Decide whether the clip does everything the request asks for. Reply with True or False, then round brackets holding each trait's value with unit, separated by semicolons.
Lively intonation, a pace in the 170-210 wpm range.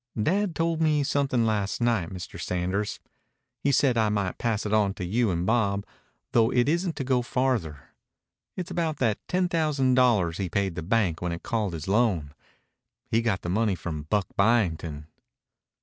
True (5.8 semitones; 180 wpm)